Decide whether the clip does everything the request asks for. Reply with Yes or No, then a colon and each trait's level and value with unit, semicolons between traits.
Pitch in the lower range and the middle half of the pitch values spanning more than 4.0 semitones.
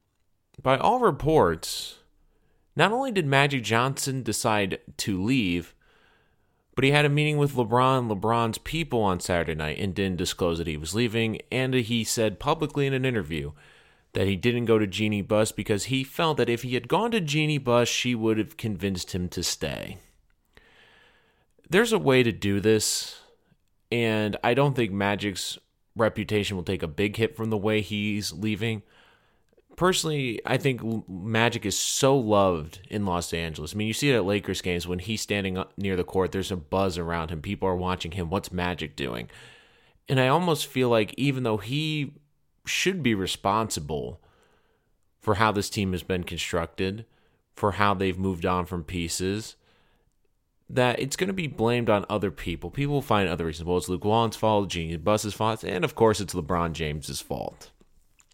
Yes: low, 105 Hz; average, 4.7 semitones